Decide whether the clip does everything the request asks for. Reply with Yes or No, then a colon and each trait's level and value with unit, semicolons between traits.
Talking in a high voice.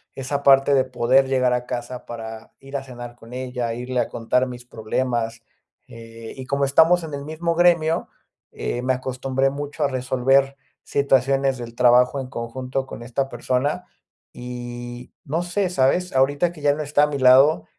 No: low, 130 Hz